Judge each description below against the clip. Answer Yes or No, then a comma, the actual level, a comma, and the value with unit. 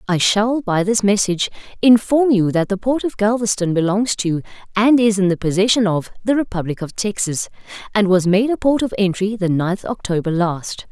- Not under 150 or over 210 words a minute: Yes, average, 200 wpm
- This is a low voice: No, high, 205 Hz